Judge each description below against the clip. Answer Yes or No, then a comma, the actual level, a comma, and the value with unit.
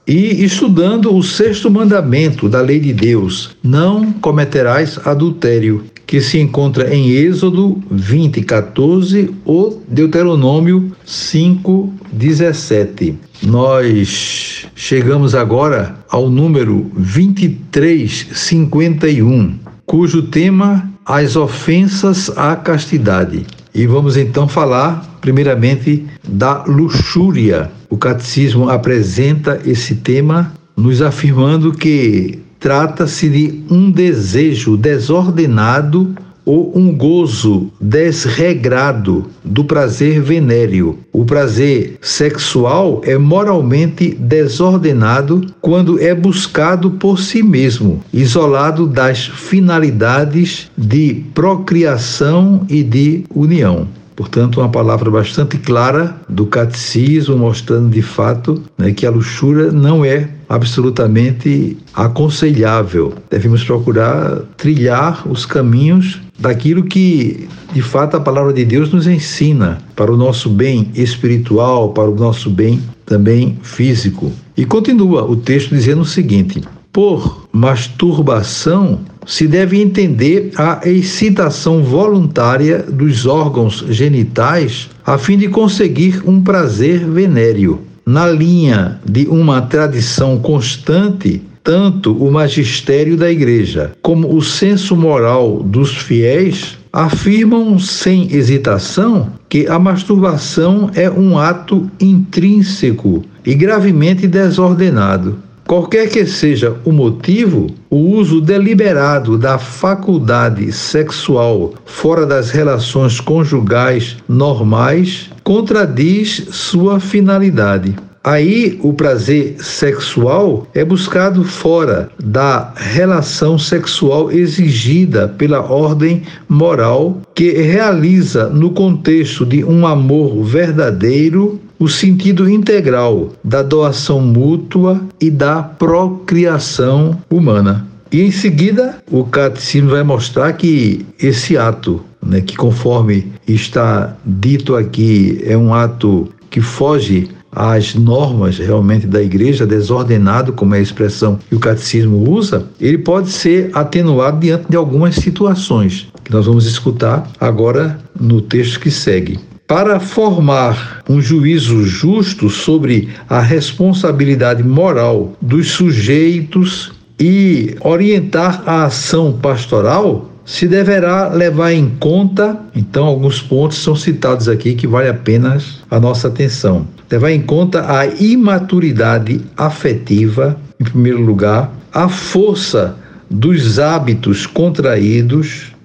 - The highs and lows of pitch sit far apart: Yes, wide, 6.2 semitones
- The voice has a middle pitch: Yes, medium, 145 Hz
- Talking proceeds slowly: Yes, slow, 105 wpm